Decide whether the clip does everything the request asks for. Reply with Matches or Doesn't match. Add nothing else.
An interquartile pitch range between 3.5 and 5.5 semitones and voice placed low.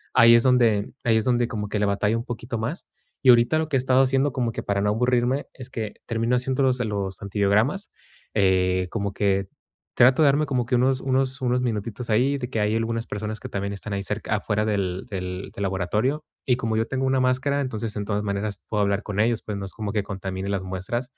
Matches